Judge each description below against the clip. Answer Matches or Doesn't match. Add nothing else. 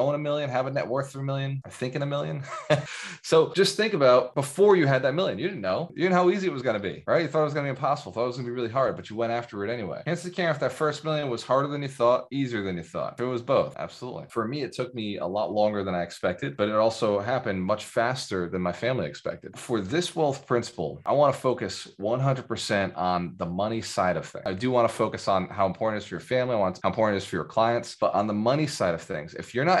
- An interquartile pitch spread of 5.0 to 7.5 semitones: Matches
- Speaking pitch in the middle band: Doesn't match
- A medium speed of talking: Doesn't match